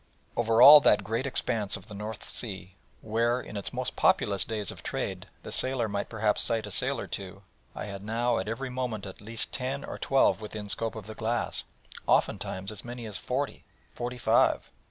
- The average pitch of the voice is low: Yes, low, 110 Hz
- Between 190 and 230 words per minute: Yes, average, 195 wpm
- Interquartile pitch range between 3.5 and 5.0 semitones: No, average, 2.9 semitones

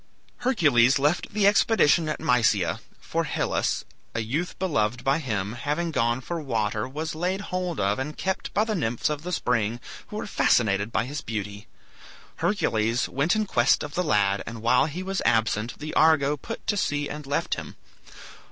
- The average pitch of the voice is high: No, medium, 140 Hz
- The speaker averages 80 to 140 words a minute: No, average, 180 wpm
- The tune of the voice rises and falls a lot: Yes, wide, 7.0 semitones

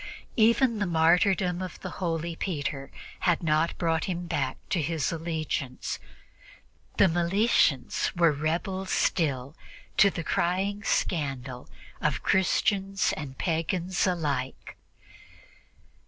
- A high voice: No, medium, 170 Hz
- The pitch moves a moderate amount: Yes, average, 3.6 semitones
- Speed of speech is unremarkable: No, slow, 110 wpm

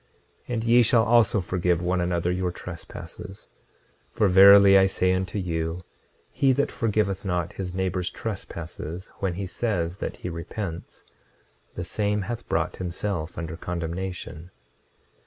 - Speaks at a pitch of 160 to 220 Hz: No, very low, 95 Hz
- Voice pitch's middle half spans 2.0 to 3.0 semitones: Yes, narrow, 2.6 semitones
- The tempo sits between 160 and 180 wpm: No, average, 140 wpm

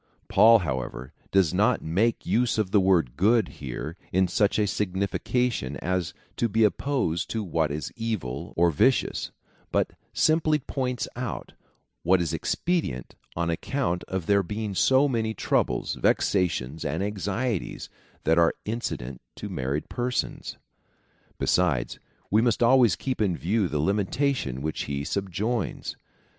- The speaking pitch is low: Yes, very low, 95 Hz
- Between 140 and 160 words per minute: Yes, average, 145 wpm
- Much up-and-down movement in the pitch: Yes, wide, 6.1 semitones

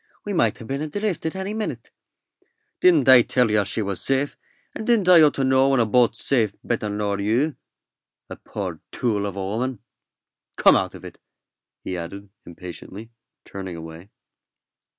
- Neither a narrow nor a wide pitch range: No, wide, 5.7 semitones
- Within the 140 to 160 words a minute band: No, average, 170 wpm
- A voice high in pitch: No, low, 115 Hz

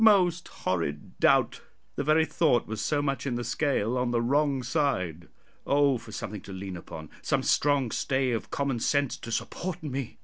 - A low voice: Yes, low, 130 Hz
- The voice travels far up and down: No, average, 4.7 semitones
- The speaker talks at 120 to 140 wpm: No, average, 180 wpm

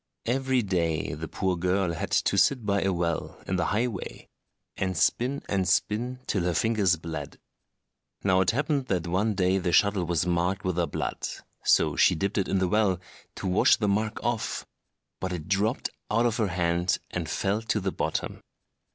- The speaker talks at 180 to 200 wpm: Yes, average, 185 wpm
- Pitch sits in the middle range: No, very low, 95 Hz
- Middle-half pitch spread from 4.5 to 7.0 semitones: No, average, 3.4 semitones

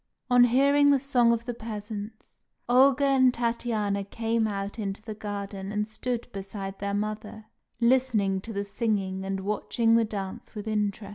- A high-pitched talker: Yes, high, 215 Hz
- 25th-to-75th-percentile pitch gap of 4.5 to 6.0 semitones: No, average, 2.9 semitones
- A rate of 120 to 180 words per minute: Yes, average, 160 wpm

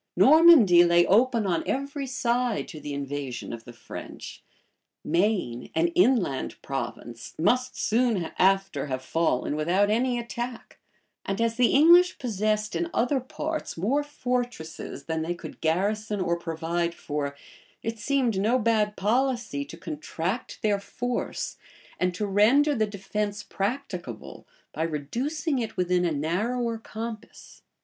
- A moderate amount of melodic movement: No, wide, 6.6 semitones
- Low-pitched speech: No, high, 205 Hz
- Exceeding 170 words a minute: No, slow, 135 wpm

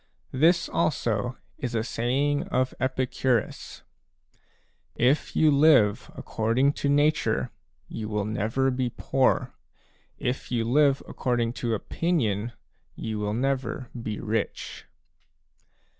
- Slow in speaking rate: Yes, slow, 115 wpm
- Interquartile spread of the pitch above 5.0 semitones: No, average, 3.4 semitones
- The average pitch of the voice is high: No, low, 125 Hz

